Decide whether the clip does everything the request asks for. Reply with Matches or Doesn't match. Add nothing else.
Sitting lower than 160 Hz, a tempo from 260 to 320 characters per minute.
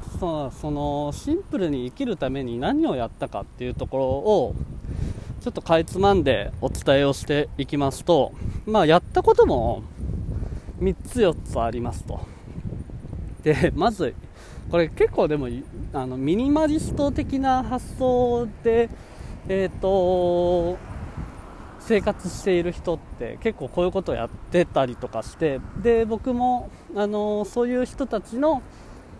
Doesn't match